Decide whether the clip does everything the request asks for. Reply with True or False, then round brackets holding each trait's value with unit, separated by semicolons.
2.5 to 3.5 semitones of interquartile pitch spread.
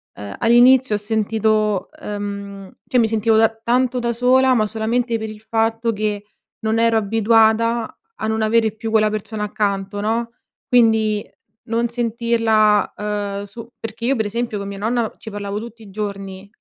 False (1.8 semitones)